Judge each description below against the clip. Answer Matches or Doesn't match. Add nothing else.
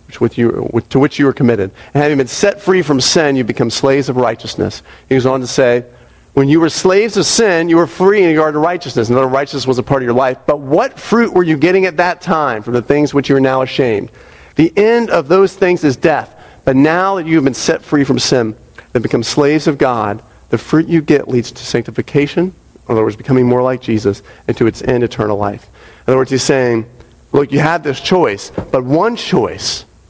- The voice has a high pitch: Doesn't match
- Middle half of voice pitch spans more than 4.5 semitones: Matches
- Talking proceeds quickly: Matches